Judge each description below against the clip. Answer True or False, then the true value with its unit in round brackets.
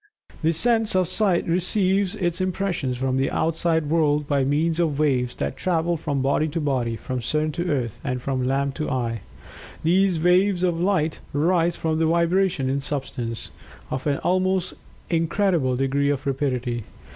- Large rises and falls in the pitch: False (4.5 semitones)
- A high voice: False (155 Hz)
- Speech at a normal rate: True (160 wpm)